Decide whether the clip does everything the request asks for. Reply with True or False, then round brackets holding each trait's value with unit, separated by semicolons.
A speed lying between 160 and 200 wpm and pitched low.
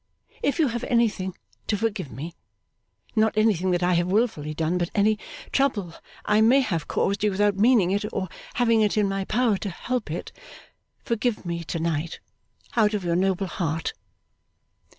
False (170 wpm; 200 Hz)